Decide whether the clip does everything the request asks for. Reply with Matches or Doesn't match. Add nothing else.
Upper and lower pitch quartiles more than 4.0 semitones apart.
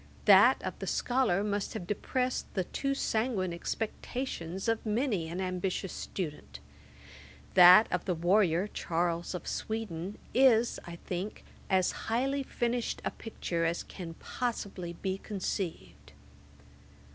Matches